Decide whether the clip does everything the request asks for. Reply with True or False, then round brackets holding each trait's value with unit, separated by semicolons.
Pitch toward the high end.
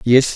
False (125 Hz)